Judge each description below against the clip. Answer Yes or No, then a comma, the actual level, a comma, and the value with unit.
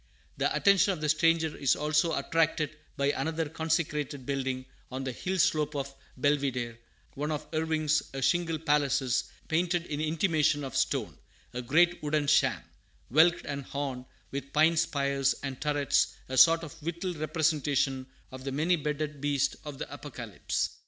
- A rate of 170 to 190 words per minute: No, average, 155 wpm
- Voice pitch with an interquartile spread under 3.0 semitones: Yes, narrow, 2.6 semitones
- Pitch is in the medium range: Yes, medium, 150 Hz